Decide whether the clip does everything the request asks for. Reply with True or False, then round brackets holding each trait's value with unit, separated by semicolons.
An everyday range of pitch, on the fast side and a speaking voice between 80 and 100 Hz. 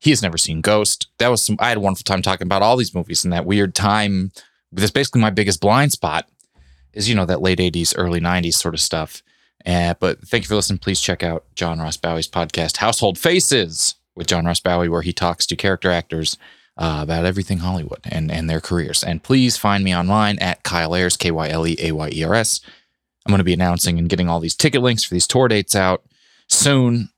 True (3.7 semitones; 235 wpm; 90 Hz)